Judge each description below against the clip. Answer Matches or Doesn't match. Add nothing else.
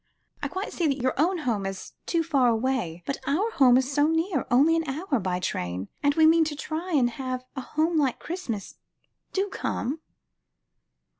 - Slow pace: Doesn't match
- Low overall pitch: Doesn't match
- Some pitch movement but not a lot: Matches